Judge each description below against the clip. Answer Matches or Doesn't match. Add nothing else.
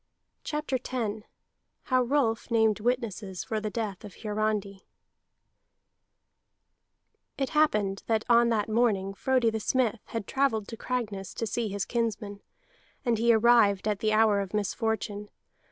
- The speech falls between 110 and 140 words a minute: Matches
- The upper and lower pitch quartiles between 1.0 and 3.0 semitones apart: Matches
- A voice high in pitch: Matches